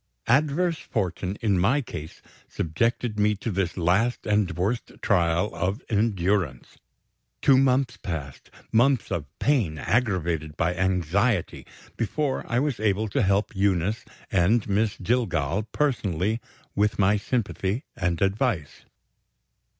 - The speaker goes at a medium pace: No, slow, 120 wpm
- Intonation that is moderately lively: Yes, average, 4.8 semitones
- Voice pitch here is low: Yes, low, 100 Hz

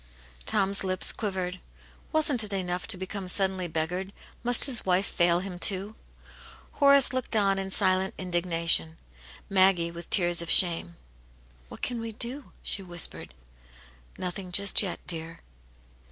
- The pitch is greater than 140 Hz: Yes, medium, 185 Hz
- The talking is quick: No, average, 145 wpm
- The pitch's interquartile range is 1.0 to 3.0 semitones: Yes, narrow, 2.5 semitones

